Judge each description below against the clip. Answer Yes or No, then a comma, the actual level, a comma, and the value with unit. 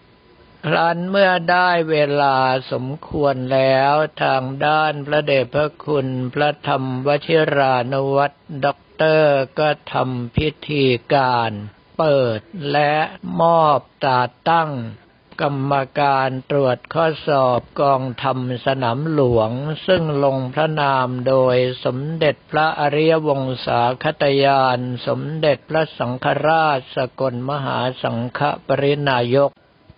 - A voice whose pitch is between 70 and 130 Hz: No, medium, 140 Hz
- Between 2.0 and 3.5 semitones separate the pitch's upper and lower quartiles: Yes, average, 2.8 semitones